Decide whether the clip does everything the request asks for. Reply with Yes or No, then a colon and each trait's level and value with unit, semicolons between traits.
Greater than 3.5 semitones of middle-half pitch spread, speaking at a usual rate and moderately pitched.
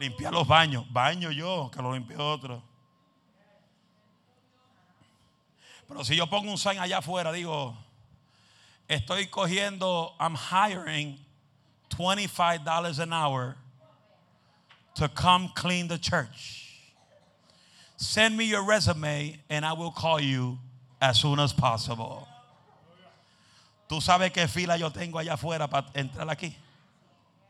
No: average, 4.5 semitones; slow, 120 wpm; medium, 150 Hz